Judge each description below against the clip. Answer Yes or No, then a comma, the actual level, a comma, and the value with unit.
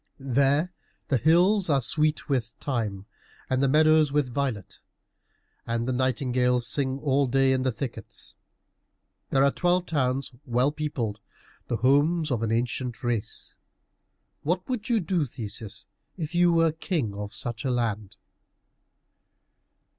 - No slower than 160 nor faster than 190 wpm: No, average, 140 wpm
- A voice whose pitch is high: No, low, 135 Hz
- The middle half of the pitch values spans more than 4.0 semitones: Yes, average, 4.4 semitones